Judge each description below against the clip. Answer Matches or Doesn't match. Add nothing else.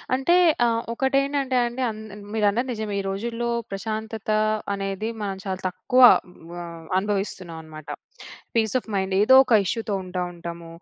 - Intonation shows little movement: Doesn't match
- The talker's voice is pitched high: Matches